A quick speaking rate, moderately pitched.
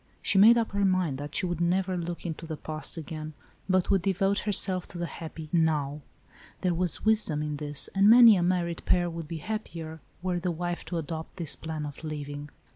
Yes: fast, 210 wpm; medium, 170 Hz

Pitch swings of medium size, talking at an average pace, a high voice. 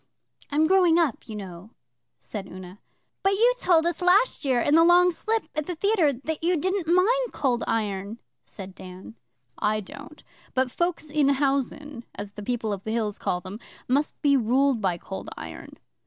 No: wide, 8.2 semitones; average, 180 wpm; very high, 280 Hz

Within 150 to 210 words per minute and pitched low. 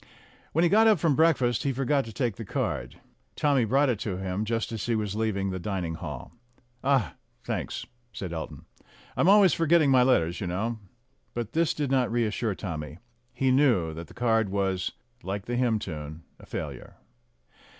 Yes: average, 180 wpm; low, 115 Hz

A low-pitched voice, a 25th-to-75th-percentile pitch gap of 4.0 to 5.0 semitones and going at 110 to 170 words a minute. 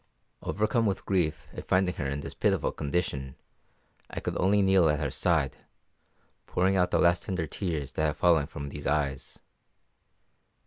Yes: very low, 80 Hz; average, 4.5 semitones; average, 165 wpm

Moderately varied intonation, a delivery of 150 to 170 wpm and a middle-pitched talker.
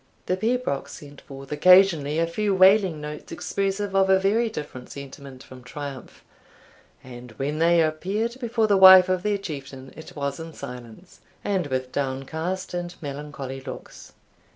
No: wide, 5.7 semitones; average, 155 wpm; medium, 160 Hz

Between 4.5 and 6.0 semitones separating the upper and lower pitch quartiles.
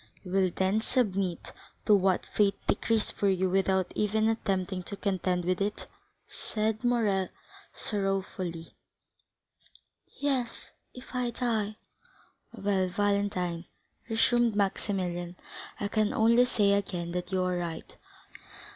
No: average, 2.9 semitones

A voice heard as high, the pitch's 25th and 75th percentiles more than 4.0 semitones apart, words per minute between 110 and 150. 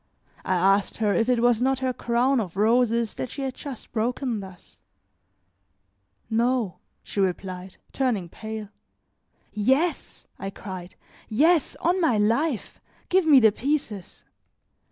Yes: high, 230 Hz; average, 4.5 semitones; slow, 135 wpm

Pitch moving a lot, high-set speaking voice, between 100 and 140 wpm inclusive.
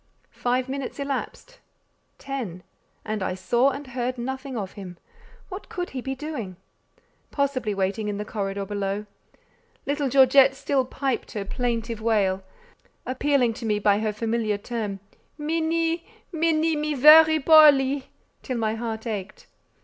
No: average, 4.9 semitones; very high, 250 Hz; slow, 135 wpm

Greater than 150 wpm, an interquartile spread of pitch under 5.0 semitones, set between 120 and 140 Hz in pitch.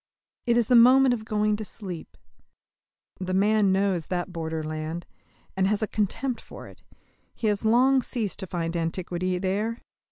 No: average, 160 wpm; average, 3.8 semitones; high, 200 Hz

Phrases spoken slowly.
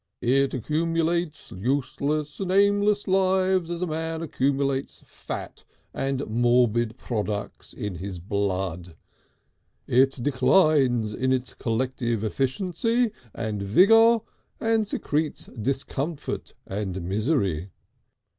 Yes: slow, 100 wpm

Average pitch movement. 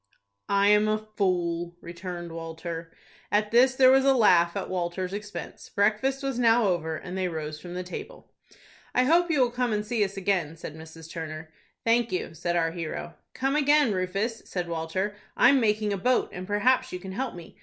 No: wide, 5.7 semitones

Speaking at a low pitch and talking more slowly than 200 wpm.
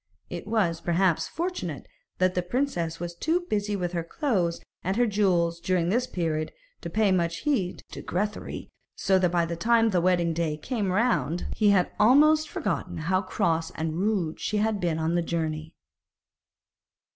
No: medium, 180 Hz; average, 170 wpm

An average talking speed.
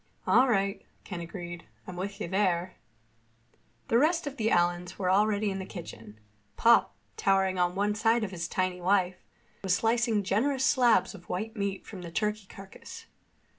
Yes: average, 170 wpm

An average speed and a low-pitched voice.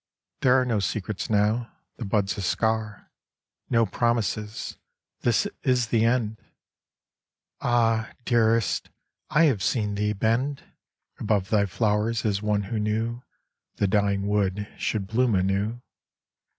No: slow, 125 wpm; low, 110 Hz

